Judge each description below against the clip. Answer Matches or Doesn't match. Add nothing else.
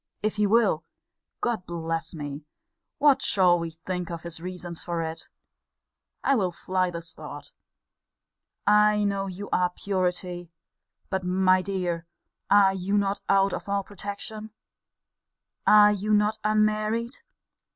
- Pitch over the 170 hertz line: Matches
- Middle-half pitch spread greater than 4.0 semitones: Doesn't match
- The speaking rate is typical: Doesn't match